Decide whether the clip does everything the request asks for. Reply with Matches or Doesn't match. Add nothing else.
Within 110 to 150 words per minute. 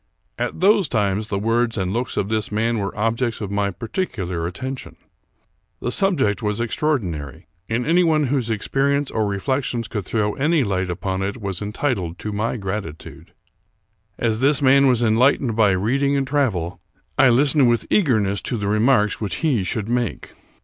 Doesn't match